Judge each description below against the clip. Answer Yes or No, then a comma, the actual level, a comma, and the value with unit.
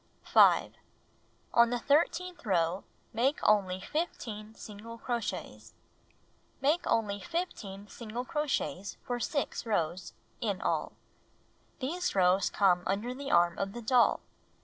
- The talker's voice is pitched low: No, high, 225 Hz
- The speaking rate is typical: No, slow, 125 wpm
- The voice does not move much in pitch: No, average, 5.2 semitones